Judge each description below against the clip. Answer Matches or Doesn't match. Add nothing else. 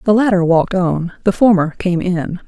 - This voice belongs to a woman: Matches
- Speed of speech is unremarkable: Matches